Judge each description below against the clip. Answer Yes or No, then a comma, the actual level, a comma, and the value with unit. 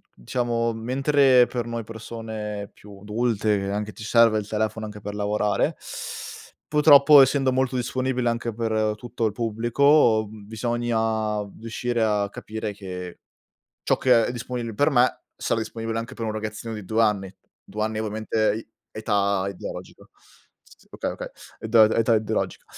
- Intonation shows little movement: Yes, narrow, 2.1 semitones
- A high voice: No, low, 110 Hz